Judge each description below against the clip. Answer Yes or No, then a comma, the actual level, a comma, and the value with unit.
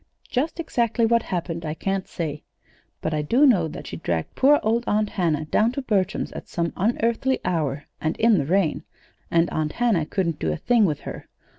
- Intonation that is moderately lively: No, wide, 6.8 semitones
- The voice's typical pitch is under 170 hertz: No, medium, 185 Hz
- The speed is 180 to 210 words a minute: Yes, average, 195 wpm